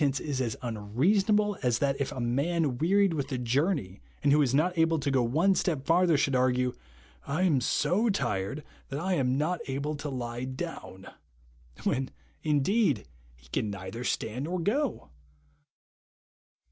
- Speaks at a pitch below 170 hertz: Yes, medium, 140 Hz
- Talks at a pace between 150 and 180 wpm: Yes, average, 165 wpm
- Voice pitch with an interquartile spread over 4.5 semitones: Yes, average, 5.3 semitones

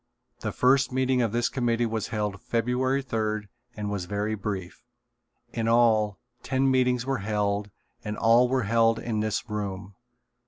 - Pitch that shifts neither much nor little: Yes, average, 3.0 semitones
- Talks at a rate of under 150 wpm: No, average, 155 wpm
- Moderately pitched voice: No, low, 115 Hz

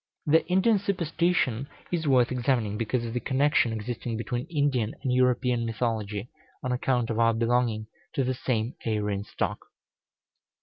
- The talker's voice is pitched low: Yes, low, 125 Hz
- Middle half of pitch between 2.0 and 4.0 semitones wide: Yes, average, 3.2 semitones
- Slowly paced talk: No, average, 145 wpm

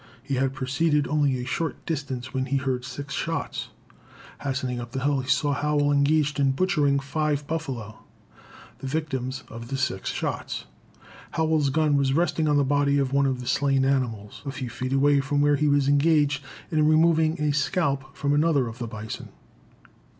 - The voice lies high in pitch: No, medium, 140 Hz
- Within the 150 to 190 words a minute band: Yes, average, 180 wpm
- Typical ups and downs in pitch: No, narrow, 2.2 semitones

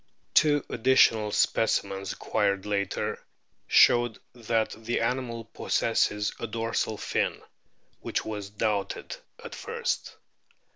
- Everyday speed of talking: No, slow, 100 wpm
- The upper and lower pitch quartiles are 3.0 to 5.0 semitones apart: No, narrow, 2.4 semitones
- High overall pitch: No, low, 110 Hz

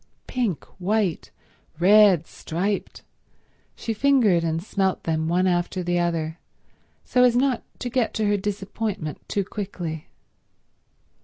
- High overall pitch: Yes, high, 195 Hz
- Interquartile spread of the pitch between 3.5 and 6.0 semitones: Yes, average, 3.9 semitones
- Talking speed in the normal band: No, slow, 120 wpm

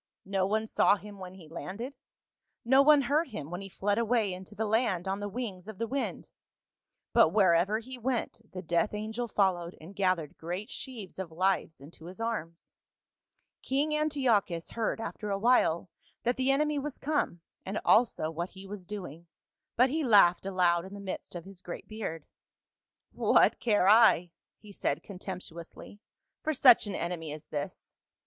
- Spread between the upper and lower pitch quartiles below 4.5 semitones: No, average, 4.8 semitones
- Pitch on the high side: Yes, high, 200 Hz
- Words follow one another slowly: No, average, 175 wpm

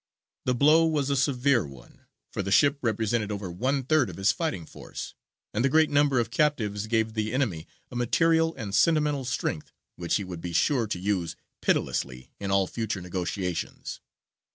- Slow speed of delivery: No, average, 175 wpm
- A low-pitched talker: Yes, low, 115 Hz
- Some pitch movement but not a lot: No, wide, 6.3 semitones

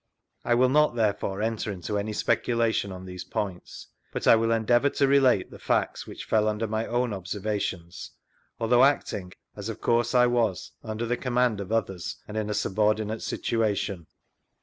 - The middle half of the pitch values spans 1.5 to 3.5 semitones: Yes, average, 2.9 semitones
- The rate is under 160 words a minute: No, average, 175 wpm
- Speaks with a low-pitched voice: Yes, low, 110 Hz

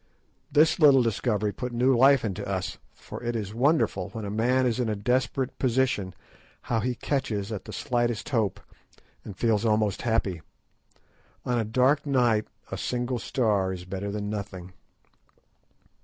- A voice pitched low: Yes, low, 115 Hz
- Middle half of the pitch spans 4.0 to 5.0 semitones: No, average, 3.6 semitones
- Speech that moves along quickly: No, average, 155 wpm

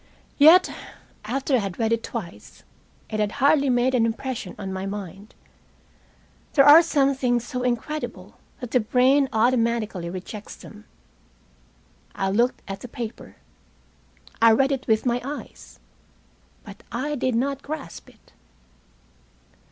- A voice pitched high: Yes, high, 240 Hz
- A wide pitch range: No, average, 4.1 semitones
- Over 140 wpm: No, slow, 135 wpm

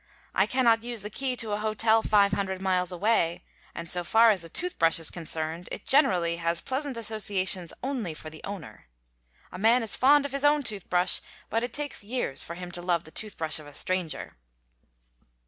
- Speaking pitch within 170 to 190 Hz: No, high, 200 Hz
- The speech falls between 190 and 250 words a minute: Yes, average, 200 wpm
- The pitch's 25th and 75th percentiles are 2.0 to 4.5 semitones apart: No, average, 5.2 semitones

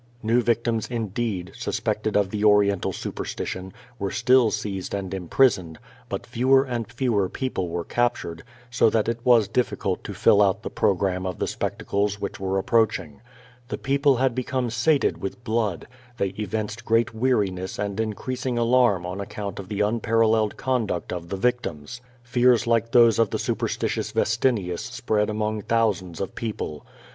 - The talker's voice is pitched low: Yes, low, 110 Hz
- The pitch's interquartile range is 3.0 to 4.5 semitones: Yes, average, 3.5 semitones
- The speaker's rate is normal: Yes, average, 165 wpm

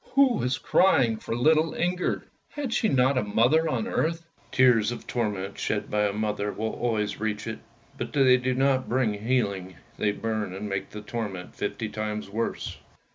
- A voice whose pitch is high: No, low, 115 Hz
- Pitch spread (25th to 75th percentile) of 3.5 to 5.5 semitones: Yes, average, 4.0 semitones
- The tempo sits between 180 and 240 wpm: Yes, average, 190 wpm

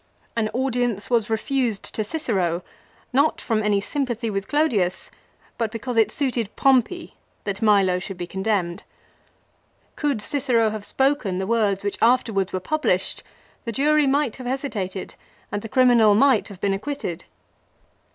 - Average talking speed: Yes, average, 150 wpm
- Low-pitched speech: No, high, 225 Hz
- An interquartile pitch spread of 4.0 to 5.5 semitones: Yes, average, 4.9 semitones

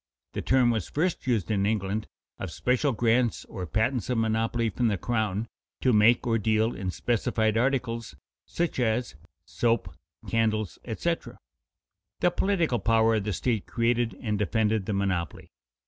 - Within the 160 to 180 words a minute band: No, average, 150 wpm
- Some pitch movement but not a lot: No, narrow, 2.3 semitones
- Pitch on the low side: Yes, low, 115 Hz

